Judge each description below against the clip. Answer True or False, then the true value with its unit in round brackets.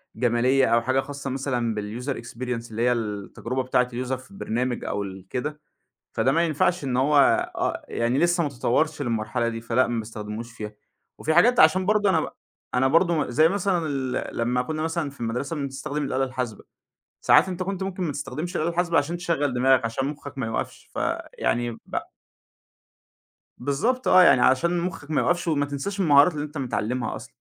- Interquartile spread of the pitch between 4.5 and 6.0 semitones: True (5.1 semitones)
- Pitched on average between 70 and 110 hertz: False (135 Hz)